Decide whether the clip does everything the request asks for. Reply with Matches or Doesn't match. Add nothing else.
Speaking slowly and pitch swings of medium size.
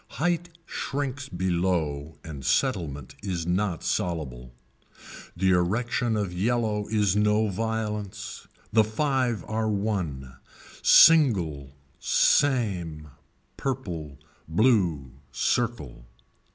Doesn't match